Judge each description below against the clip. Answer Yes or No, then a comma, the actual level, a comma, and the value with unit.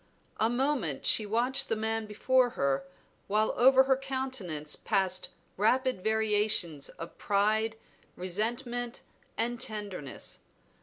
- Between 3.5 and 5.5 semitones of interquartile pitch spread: Yes, average, 4.0 semitones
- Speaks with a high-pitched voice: Yes, high, 220 Hz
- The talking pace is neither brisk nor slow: No, slow, 110 wpm